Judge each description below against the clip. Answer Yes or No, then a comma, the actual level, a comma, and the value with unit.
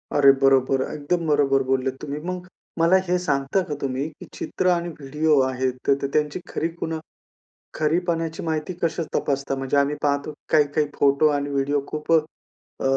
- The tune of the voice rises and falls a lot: No, average, 2.8 semitones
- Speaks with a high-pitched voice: No, medium, 145 Hz